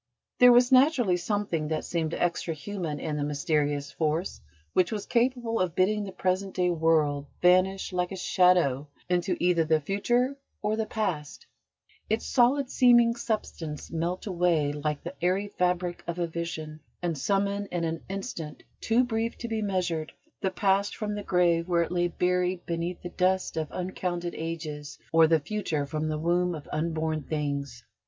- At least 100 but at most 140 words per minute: No, average, 170 wpm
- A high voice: No, medium, 175 Hz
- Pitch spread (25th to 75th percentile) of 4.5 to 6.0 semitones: No, average, 3.9 semitones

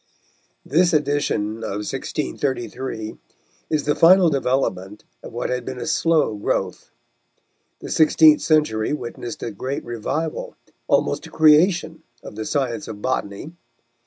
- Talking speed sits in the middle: No, slow, 130 wpm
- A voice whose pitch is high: No, low, 135 Hz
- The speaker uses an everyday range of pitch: No, wide, 5.7 semitones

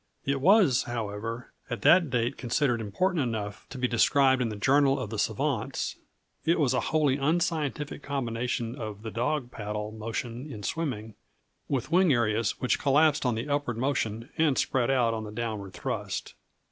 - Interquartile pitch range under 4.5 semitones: Yes, average, 4.1 semitones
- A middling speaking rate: Yes, average, 170 wpm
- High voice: No, low, 125 Hz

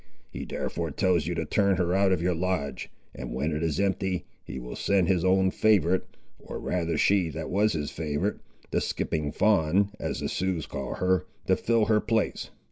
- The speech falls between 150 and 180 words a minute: No, average, 195 wpm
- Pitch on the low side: Yes, very low, 90 Hz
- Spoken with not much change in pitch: No, average, 3.3 semitones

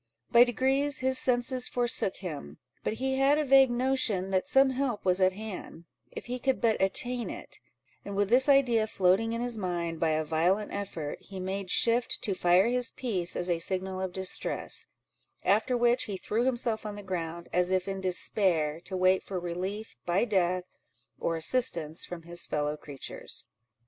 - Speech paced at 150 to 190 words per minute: Yes, average, 180 wpm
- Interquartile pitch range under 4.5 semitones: No, average, 5.3 semitones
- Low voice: No, high, 195 Hz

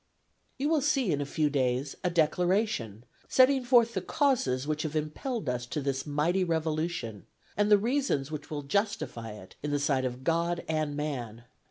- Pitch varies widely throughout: Yes, wide, 6.9 semitones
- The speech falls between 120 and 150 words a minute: No, average, 180 wpm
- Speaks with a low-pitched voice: No, medium, 155 Hz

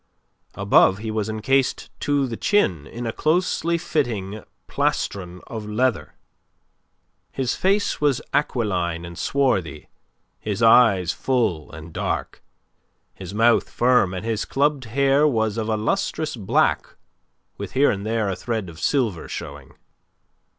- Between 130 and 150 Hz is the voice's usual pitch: No, low, 115 Hz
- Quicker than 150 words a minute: No, slow, 135 wpm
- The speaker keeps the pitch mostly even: No, wide, 5.6 semitones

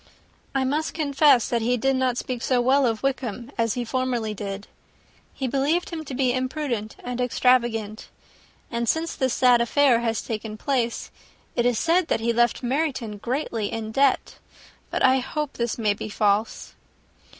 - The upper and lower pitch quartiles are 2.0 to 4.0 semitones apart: Yes, average, 2.9 semitones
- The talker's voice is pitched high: Yes, high, 245 Hz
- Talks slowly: No, average, 170 wpm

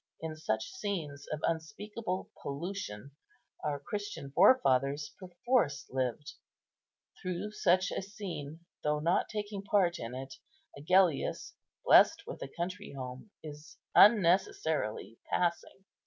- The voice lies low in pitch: No, medium, 165 Hz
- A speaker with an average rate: No, slow, 110 wpm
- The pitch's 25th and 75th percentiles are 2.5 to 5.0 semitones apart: No, wide, 5.5 semitones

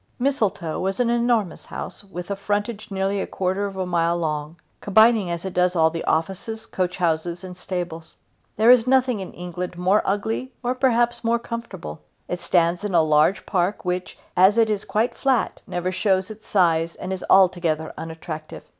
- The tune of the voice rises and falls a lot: No, average, 4.0 semitones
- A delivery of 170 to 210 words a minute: Yes, average, 180 wpm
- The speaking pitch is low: No, high, 190 Hz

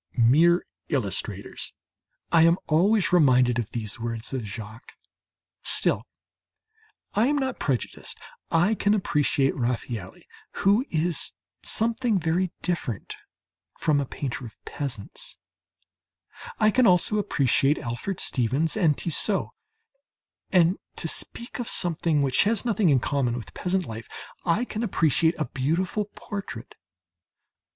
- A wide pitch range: Yes, wide, 7.5 semitones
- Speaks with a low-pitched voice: No, medium, 160 Hz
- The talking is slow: Yes, slow, 125 wpm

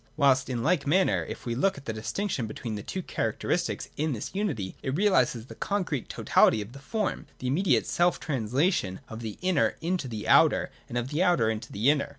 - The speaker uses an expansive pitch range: Yes, wide, 7.3 semitones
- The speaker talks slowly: No, average, 180 wpm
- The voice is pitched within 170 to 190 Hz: No, medium, 140 Hz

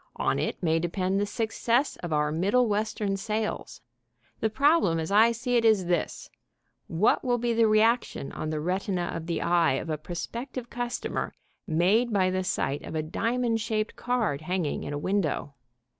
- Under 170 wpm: No, average, 175 wpm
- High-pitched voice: Yes, high, 200 Hz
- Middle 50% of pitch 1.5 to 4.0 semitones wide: No, wide, 5.4 semitones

